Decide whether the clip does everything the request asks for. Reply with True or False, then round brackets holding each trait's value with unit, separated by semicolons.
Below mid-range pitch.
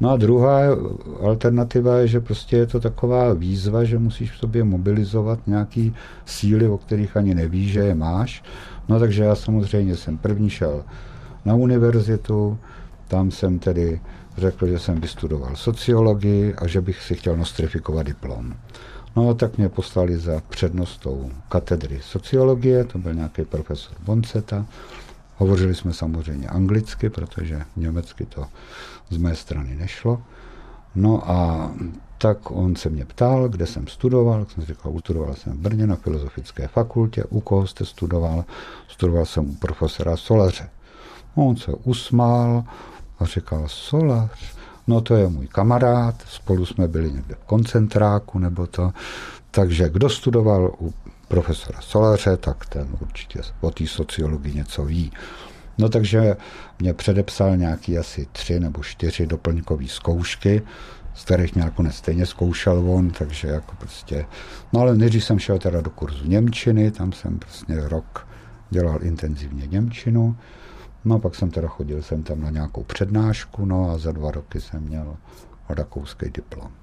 True (95 Hz)